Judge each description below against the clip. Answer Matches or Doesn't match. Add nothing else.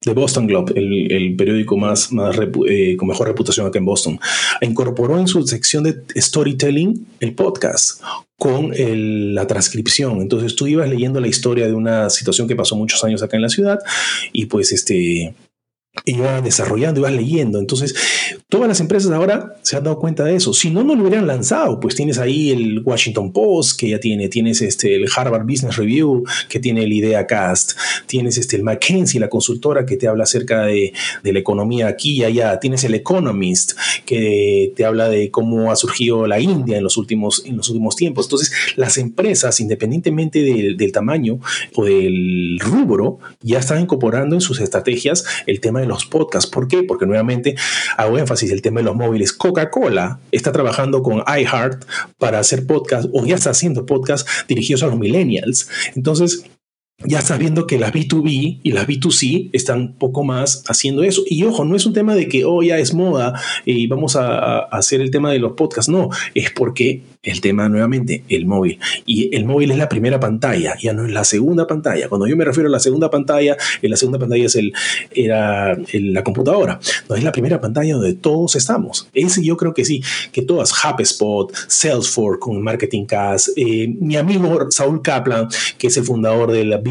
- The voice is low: Matches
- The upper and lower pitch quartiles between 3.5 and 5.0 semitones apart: Doesn't match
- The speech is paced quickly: Matches